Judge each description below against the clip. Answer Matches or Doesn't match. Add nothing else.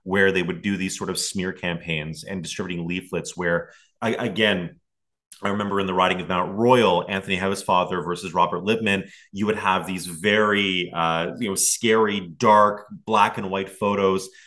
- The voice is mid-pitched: Doesn't match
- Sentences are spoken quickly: Doesn't match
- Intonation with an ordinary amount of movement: Doesn't match